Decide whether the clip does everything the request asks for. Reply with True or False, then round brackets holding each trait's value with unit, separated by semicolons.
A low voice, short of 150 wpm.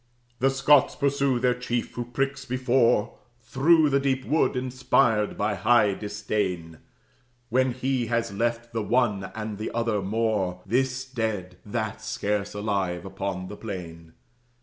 True (115 Hz; 140 wpm)